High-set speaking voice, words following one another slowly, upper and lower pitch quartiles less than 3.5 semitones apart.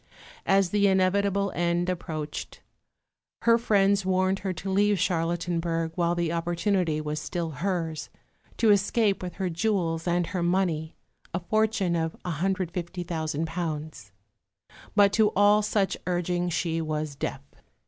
No: medium, 175 Hz; slow, 130 wpm; average, 2.9 semitones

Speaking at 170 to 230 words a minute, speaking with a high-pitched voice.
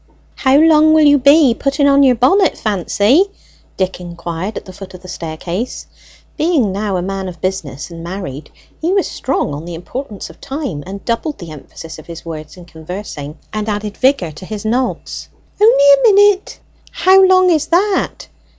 Yes: average, 180 wpm; high, 210 Hz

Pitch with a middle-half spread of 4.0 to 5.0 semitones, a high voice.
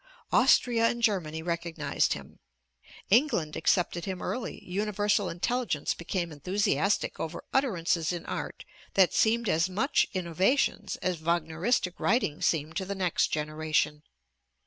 No: average, 4.5 semitones; medium, 180 Hz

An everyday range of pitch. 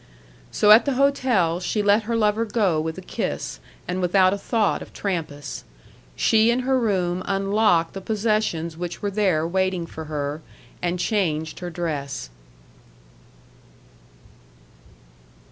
Yes: average, 4.4 semitones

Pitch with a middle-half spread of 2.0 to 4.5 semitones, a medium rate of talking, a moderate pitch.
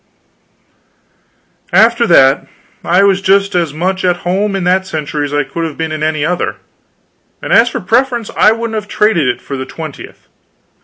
No: average, 5.2 semitones; average, 175 wpm; medium, 180 Hz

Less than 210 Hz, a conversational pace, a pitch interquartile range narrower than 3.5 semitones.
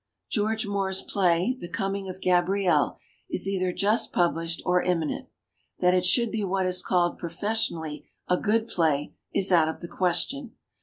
Yes: medium, 185 Hz; average, 170 wpm; narrow, 2.6 semitones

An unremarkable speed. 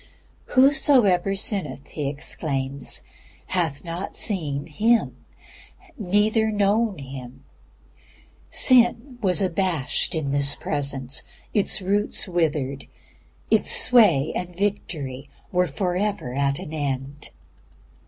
No: slow, 95 wpm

